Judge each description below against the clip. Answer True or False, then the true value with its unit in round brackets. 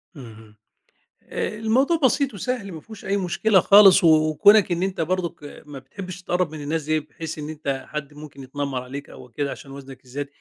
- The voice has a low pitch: False (155 Hz)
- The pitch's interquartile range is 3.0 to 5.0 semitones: False (5.5 semitones)